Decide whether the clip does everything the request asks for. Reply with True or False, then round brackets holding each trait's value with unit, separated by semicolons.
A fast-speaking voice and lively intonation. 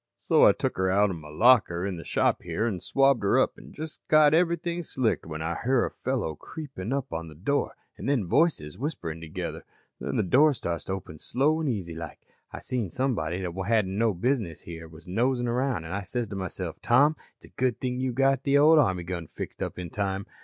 True (225 wpm; 7.6 semitones)